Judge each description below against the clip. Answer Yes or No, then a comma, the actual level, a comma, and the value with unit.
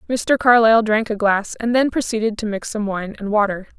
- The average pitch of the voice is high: Yes, high, 220 Hz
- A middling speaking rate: No, fast, 220 wpm